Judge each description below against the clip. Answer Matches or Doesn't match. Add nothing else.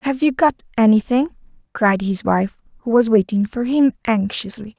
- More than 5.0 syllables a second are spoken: Doesn't match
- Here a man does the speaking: Doesn't match